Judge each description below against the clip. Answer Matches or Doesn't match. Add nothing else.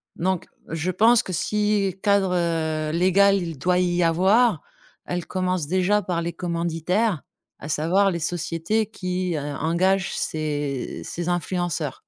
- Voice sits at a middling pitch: Matches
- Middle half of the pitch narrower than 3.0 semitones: Matches